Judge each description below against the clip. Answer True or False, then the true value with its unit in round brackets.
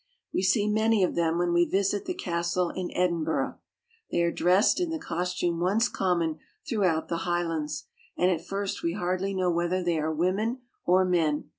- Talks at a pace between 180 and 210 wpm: True (190 wpm)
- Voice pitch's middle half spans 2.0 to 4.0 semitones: True (2.4 semitones)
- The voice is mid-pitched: True (180 Hz)